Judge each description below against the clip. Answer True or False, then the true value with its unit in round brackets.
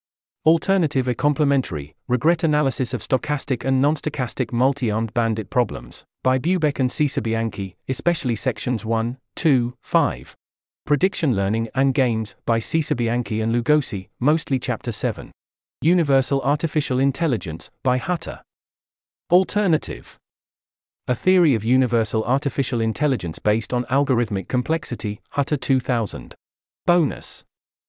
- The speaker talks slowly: True (115 wpm)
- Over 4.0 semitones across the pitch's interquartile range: True (4.7 semitones)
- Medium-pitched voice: False (125 Hz)